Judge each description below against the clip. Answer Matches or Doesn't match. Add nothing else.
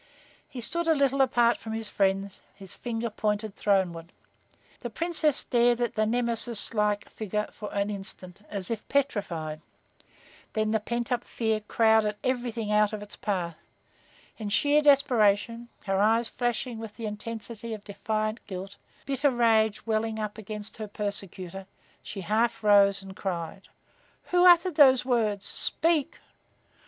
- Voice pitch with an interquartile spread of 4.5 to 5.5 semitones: Doesn't match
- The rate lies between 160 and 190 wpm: Doesn't match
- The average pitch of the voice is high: Matches